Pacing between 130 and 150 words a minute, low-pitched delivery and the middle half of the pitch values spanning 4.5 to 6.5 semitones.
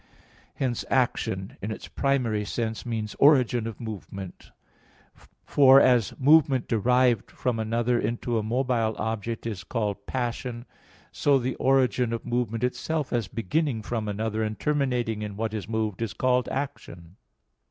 No: average, 140 wpm; low, 115 Hz; average, 2.8 semitones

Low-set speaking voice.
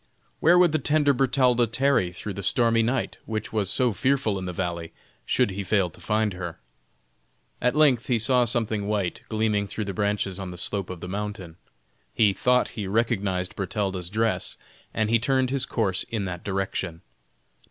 Yes: low, 105 Hz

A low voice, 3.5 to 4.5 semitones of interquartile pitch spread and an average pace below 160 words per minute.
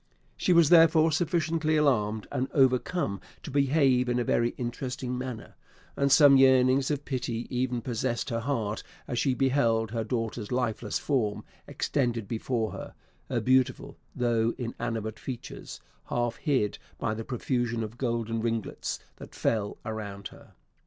No: low, 125 Hz; average, 3.1 semitones; average, 145 wpm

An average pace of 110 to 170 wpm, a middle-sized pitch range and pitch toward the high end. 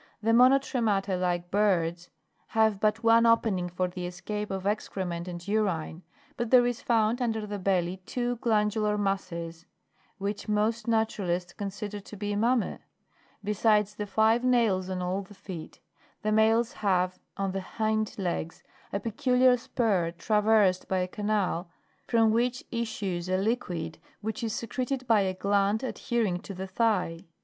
Yes: average, 150 wpm; average, 3.3 semitones; high, 210 Hz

